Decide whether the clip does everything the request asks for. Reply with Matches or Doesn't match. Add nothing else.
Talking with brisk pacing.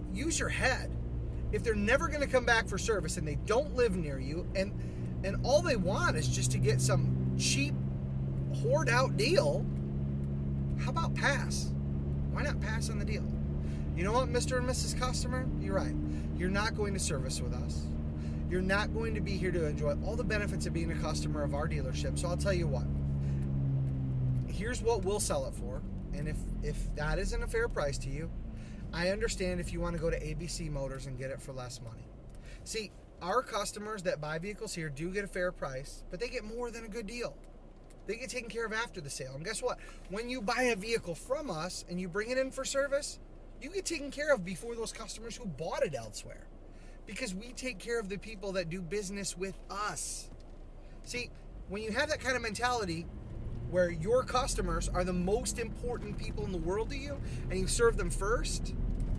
Matches